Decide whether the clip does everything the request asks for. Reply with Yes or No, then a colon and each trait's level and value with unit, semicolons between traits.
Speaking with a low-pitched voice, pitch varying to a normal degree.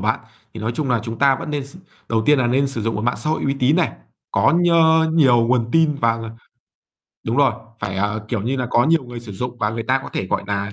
Yes: low, 120 Hz; average, 4.0 semitones